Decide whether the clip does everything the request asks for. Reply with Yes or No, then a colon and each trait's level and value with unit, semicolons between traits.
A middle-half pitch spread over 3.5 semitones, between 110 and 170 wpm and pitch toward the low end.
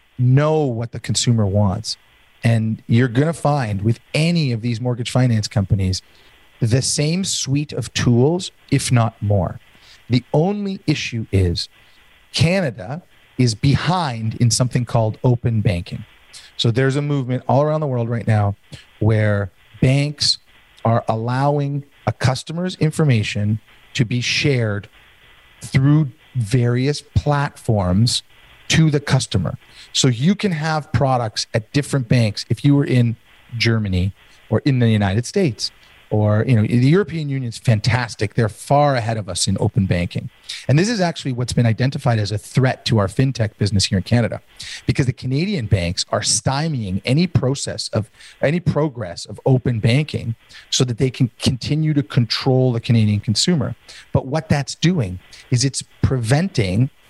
Yes: average, 4.4 semitones; average, 150 wpm; low, 125 Hz